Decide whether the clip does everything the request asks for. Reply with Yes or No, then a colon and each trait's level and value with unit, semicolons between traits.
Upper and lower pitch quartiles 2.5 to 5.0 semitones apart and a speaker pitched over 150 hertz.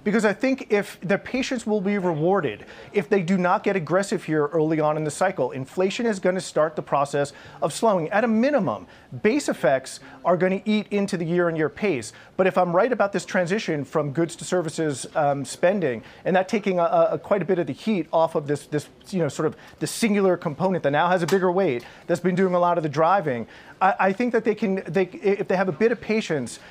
Yes: average, 4.0 semitones; medium, 185 Hz